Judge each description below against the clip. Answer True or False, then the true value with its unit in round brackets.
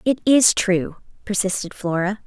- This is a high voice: True (200 Hz)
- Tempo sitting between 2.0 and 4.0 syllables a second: False (4.4 syllables/s)